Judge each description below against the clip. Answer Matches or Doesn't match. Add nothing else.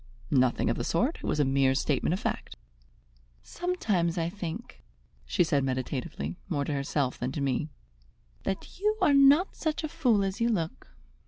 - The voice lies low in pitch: Doesn't match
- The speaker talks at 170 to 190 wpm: Matches